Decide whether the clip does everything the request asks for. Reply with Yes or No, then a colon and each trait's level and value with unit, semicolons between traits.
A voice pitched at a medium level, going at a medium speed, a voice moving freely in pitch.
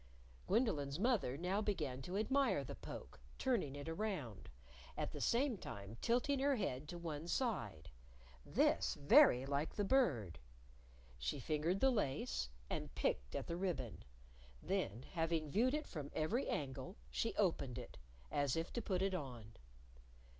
Yes: medium, 165 Hz; average, 150 wpm; wide, 8.5 semitones